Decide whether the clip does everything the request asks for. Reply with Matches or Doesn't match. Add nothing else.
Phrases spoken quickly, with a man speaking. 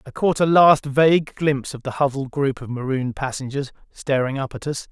Matches